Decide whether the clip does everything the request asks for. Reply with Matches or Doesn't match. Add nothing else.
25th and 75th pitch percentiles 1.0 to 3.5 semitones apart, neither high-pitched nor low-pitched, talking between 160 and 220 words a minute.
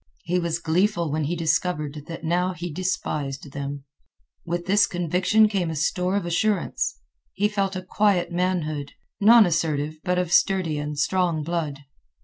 Doesn't match